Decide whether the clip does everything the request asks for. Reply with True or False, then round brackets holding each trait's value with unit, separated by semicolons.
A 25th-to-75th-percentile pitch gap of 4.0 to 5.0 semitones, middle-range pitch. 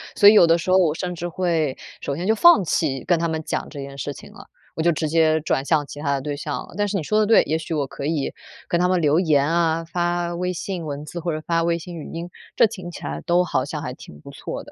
False (3.0 semitones; 165 Hz)